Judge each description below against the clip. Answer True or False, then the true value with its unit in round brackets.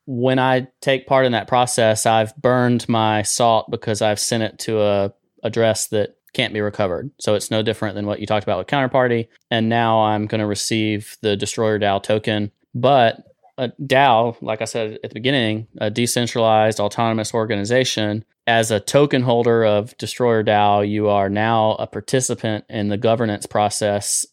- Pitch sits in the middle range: False (110 Hz)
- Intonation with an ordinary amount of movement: False (2.2 semitones)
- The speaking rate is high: False (180 wpm)